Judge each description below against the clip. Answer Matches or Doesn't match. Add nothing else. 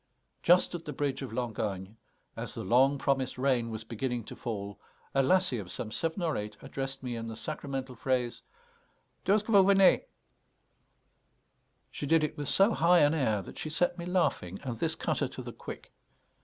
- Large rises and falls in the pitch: Matches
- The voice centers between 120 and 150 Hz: Matches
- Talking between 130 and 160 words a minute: Doesn't match